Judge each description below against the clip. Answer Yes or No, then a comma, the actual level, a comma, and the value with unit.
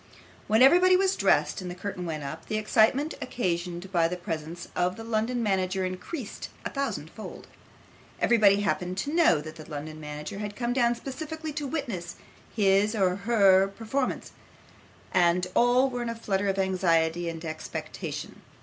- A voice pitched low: No, high, 195 Hz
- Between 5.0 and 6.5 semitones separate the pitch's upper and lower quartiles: Yes, wide, 5.4 semitones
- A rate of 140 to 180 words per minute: Yes, average, 170 wpm